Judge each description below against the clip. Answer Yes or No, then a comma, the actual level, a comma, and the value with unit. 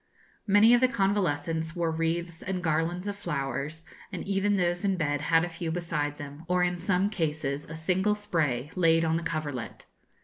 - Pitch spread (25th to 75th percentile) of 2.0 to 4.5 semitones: Yes, average, 3.0 semitones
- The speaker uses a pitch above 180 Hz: No, medium, 165 Hz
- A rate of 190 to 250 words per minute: No, average, 180 wpm